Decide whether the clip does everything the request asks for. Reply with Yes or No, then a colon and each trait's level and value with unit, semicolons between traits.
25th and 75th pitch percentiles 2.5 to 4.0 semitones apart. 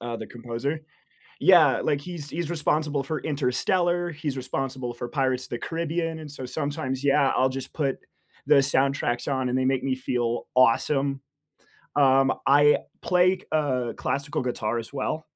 Yes: average, 2.9 semitones